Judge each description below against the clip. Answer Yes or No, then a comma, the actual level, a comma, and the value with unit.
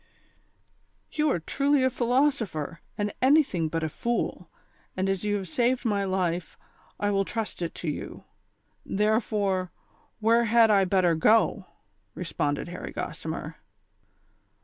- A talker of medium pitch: No, high, 205 Hz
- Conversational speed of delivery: Yes, average, 150 wpm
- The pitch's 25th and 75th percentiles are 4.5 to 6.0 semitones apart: Yes, average, 5.0 semitones